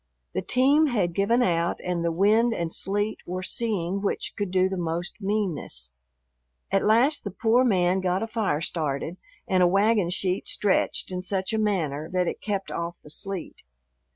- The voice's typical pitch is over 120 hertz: Yes, high, 190 Hz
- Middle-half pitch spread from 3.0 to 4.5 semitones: Yes, average, 3.6 semitones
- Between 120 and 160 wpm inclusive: No, average, 180 wpm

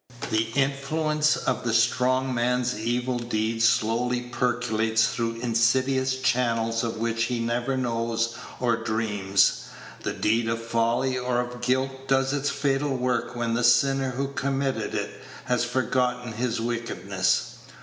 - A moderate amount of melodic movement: No, narrow, 2.2 semitones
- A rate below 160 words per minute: Yes, average, 140 wpm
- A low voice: Yes, low, 120 Hz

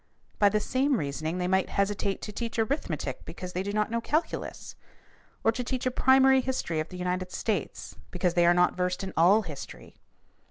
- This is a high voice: Yes, high, 200 Hz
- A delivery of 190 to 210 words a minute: Yes, average, 195 wpm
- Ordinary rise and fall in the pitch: Yes, average, 4.5 semitones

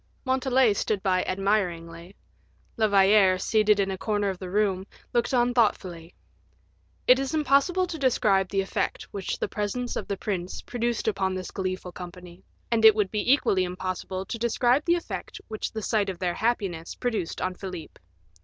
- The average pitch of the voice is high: Yes, high, 200 Hz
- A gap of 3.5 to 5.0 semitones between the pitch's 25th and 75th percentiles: Yes, average, 4.2 semitones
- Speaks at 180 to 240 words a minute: No, average, 170 wpm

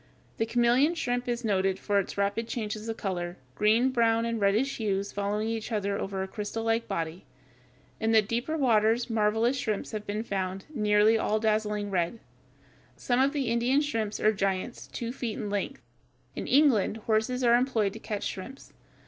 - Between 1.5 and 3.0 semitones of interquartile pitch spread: Yes, average, 2.7 semitones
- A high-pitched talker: Yes, high, 220 Hz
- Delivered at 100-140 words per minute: No, average, 180 wpm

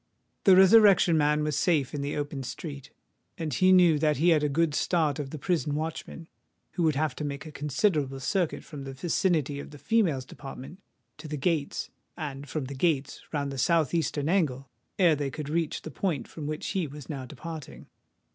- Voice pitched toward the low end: No, medium, 150 Hz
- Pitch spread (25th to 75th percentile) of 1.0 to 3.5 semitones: Yes, average, 2.9 semitones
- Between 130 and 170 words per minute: No, average, 200 wpm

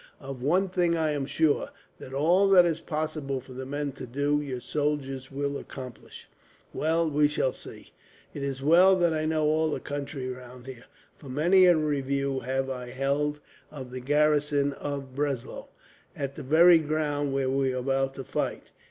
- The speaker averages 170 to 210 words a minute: Yes, average, 180 wpm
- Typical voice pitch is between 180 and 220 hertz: No, medium, 145 Hz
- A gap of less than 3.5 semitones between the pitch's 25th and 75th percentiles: Yes, narrow, 2.5 semitones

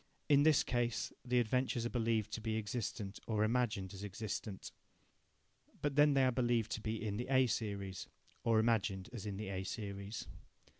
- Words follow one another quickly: No, average, 180 wpm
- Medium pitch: No, low, 110 Hz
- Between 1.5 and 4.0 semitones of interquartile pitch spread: Yes, average, 3.2 semitones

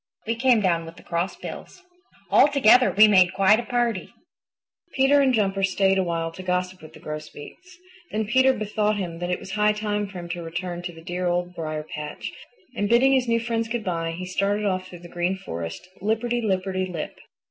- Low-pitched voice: No, high, 190 Hz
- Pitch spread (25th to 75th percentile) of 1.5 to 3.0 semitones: No, average, 4.1 semitones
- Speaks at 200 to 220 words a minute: Yes, fast, 205 wpm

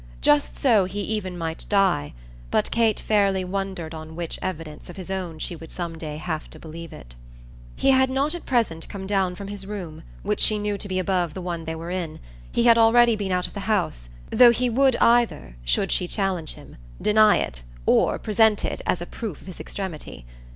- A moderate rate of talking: No, fast, 210 wpm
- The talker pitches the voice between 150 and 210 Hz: Yes, high, 190 Hz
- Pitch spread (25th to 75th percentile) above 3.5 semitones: Yes, average, 4.5 semitones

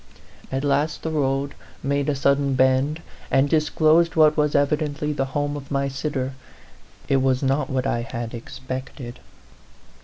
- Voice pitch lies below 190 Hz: Yes, medium, 140 Hz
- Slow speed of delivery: No, average, 155 wpm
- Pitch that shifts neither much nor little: No, narrow, 2.1 semitones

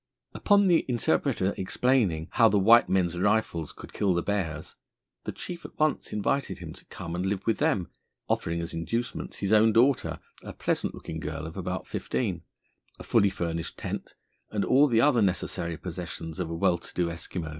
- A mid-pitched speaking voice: No, very low, 95 Hz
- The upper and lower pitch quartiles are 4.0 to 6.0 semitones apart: Yes, wide, 5.4 semitones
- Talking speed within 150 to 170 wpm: No, average, 185 wpm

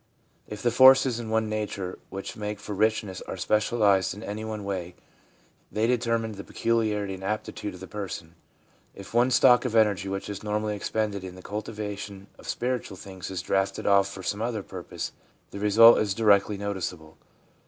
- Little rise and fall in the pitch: Yes, narrow, 2.2 semitones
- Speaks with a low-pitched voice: Yes, low, 105 Hz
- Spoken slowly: No, average, 175 wpm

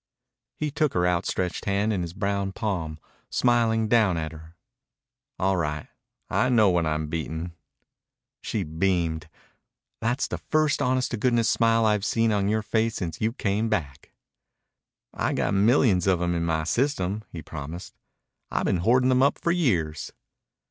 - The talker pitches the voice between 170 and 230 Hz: No, low, 100 Hz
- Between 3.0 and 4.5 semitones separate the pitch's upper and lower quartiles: No, average, 5.3 semitones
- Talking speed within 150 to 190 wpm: Yes, average, 160 wpm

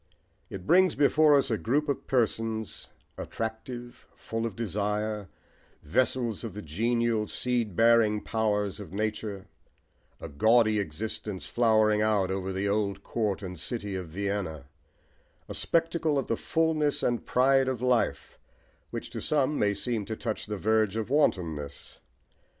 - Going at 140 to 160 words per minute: Yes, average, 145 wpm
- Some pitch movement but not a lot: Yes, average, 3.3 semitones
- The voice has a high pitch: No, low, 110 Hz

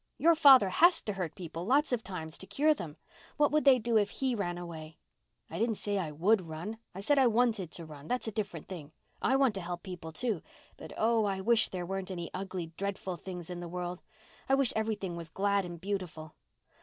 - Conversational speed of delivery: No, fast, 220 wpm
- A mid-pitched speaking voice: No, high, 195 Hz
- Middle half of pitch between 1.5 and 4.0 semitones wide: No, average, 4.6 semitones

